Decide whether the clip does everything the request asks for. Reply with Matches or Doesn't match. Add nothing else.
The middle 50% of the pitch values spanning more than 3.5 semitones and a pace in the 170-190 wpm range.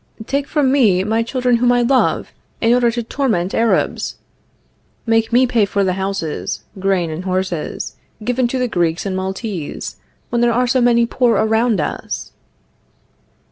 Doesn't match